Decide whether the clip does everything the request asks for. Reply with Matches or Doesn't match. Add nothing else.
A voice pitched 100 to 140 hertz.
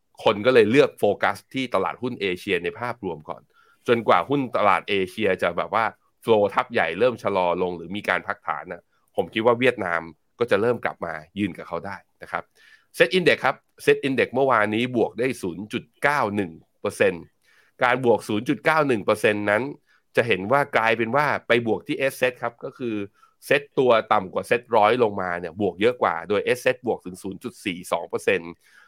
Matches